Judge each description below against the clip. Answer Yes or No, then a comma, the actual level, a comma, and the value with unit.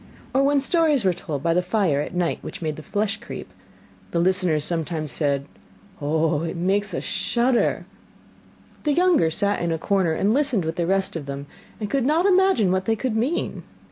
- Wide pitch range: Yes, wide, 6.8 semitones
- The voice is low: No, high, 190 Hz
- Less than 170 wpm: No, average, 195 wpm